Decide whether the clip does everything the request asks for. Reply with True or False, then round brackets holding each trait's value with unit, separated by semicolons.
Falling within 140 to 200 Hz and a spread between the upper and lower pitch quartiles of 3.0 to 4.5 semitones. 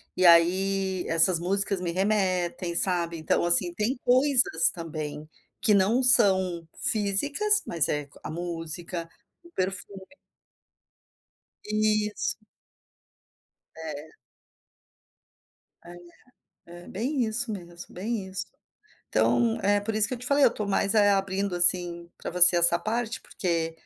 True (190 Hz; 3.8 semitones)